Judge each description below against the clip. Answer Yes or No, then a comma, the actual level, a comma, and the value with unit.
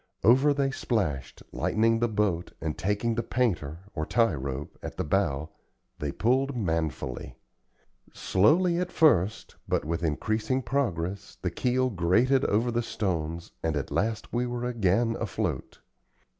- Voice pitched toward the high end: No, low, 105 Hz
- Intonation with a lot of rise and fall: Yes, wide, 6.6 semitones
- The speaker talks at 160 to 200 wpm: No, average, 145 wpm